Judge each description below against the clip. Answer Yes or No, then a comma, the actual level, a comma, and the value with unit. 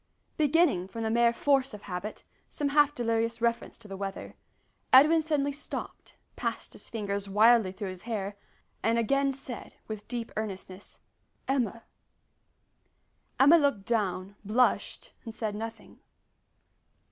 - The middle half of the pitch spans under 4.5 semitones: No, average, 4.8 semitones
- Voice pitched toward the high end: Yes, high, 230 Hz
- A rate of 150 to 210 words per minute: No, slow, 135 wpm